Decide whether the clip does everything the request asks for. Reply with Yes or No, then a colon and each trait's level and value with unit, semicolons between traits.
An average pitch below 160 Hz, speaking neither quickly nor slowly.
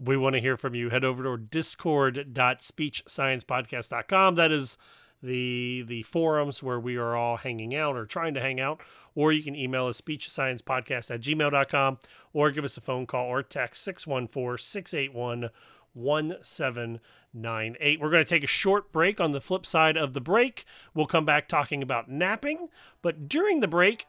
Yes: medium, 140 Hz; average, 165 wpm